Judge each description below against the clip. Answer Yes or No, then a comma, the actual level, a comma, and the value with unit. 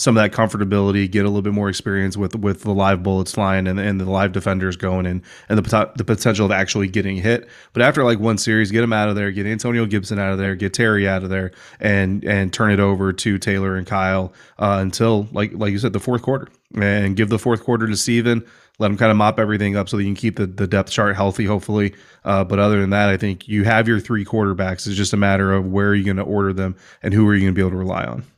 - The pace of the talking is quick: Yes, fast, 275 wpm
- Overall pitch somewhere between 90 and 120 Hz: Yes, low, 100 Hz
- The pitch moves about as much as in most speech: No, narrow, 1.9 semitones